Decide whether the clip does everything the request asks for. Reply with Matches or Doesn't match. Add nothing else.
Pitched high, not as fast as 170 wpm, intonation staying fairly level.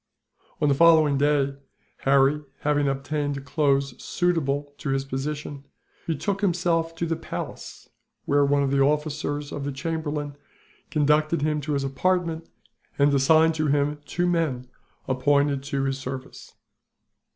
Doesn't match